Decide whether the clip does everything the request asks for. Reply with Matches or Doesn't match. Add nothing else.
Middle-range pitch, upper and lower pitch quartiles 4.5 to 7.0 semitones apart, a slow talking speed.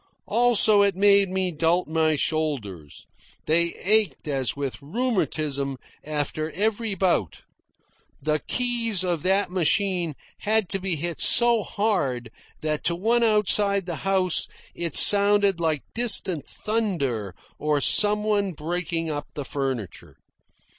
Matches